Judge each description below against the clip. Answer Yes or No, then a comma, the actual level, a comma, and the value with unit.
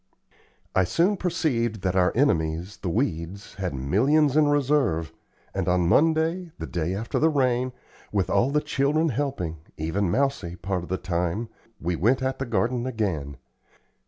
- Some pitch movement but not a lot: No, wide, 8.0 semitones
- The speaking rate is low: No, average, 160 wpm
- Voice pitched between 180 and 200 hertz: No, low, 110 Hz